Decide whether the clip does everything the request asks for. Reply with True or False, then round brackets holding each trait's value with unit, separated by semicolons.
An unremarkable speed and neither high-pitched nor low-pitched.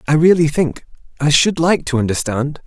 True (180 wpm; 150 Hz)